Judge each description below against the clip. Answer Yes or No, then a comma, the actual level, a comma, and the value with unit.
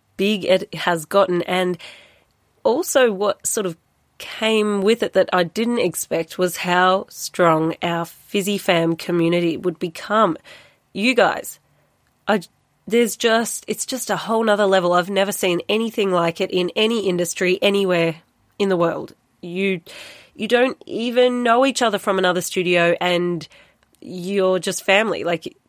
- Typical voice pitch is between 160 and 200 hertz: Yes, high, 190 Hz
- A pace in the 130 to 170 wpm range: Yes, average, 150 wpm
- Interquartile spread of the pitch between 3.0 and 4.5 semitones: Yes, average, 3.4 semitones